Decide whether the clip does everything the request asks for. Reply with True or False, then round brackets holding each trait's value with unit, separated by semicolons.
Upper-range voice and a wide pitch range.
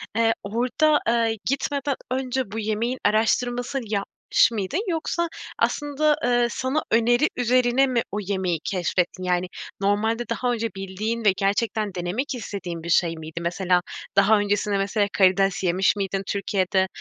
False (215 Hz; 4.1 semitones)